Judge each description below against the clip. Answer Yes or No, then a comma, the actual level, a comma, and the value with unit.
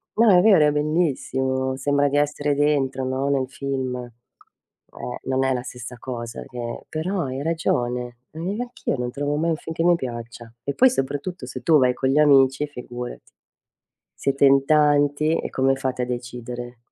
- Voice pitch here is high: No, low, 135 Hz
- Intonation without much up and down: No, average, 3.0 semitones